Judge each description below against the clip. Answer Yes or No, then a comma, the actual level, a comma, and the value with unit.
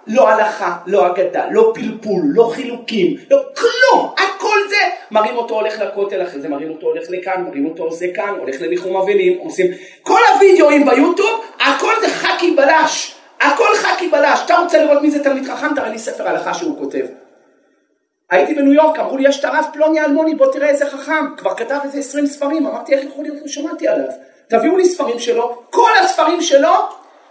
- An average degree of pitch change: No, wide, 6.5 semitones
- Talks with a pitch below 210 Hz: No, very high, 290 Hz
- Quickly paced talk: Yes, fast, 180 wpm